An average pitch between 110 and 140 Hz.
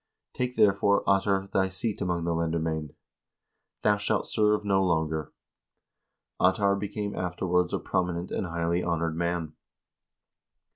No: very low, 90 Hz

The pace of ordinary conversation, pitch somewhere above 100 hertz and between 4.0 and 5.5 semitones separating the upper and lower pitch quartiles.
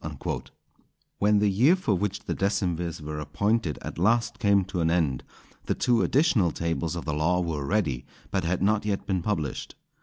No: average, 185 wpm; very low, 95 Hz; average, 4.3 semitones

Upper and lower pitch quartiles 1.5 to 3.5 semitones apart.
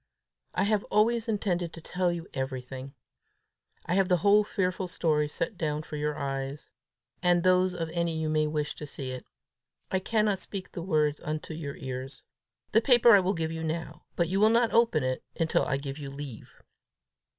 No: average, 4.2 semitones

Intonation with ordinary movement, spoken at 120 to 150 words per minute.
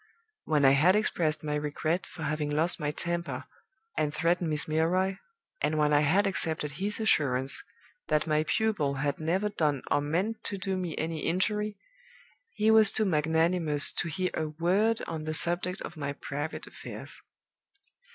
No: average, 3.7 semitones; average, 165 wpm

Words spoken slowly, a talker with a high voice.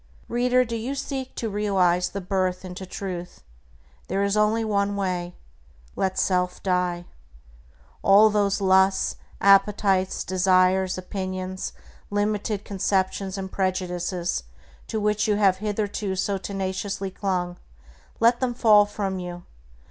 Yes: slow, 125 wpm; high, 195 Hz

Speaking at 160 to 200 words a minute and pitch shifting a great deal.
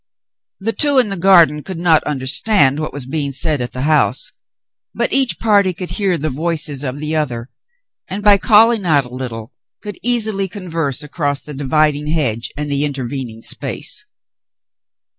Yes: average, 165 wpm; wide, 5.8 semitones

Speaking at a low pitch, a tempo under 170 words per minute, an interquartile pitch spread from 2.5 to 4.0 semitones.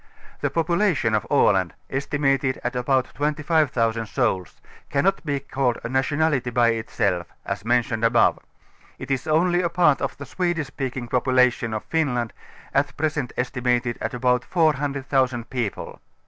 Yes: low, 130 Hz; average, 140 wpm; average, 3.5 semitones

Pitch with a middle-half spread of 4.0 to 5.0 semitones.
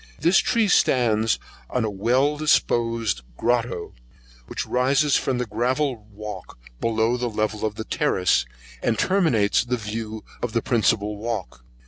No: average, 2.9 semitones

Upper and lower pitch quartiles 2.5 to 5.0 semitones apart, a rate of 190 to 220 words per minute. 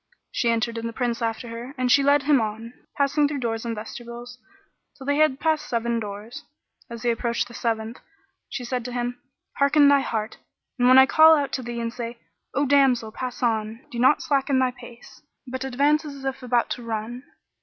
Yes: average, 2.8 semitones; fast, 205 wpm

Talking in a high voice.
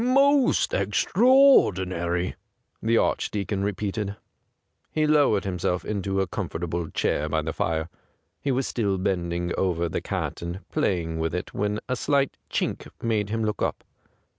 No: very low, 95 Hz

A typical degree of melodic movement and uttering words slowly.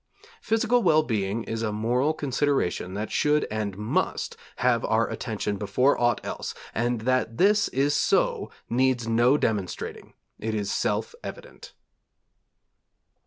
Yes: average, 4.8 semitones; slow, 130 wpm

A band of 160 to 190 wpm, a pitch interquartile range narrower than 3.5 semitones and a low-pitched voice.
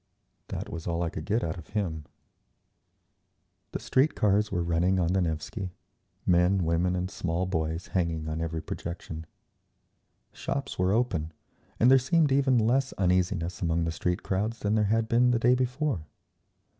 No: average, 165 wpm; wide, 5.4 semitones; very low, 90 Hz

